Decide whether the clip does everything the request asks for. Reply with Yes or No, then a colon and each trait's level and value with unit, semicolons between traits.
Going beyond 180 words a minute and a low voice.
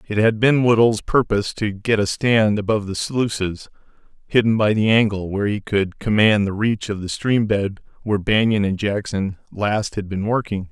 Yes: average, 190 wpm; low, 105 Hz